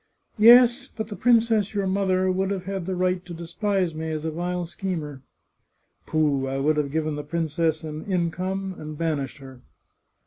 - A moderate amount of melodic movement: Yes, average, 3.8 semitones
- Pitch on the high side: No, medium, 175 Hz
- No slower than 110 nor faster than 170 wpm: No, average, 185 wpm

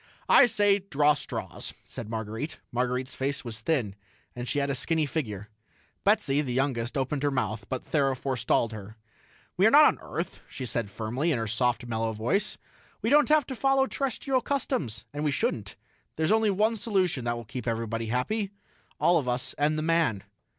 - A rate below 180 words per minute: No, average, 185 wpm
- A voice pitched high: No, low, 135 Hz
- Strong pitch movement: Yes, wide, 7.3 semitones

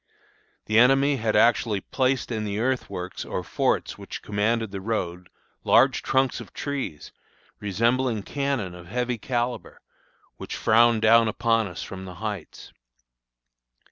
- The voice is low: Yes, low, 115 Hz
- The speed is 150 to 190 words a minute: No, slow, 135 wpm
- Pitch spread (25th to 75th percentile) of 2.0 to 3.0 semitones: No, average, 3.5 semitones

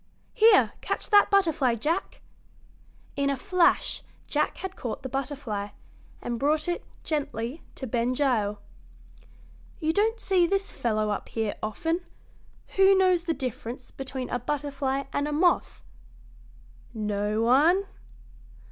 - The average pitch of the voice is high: Yes, very high, 280 Hz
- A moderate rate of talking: No, slow, 130 wpm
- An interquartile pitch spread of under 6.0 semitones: No, wide, 6.6 semitones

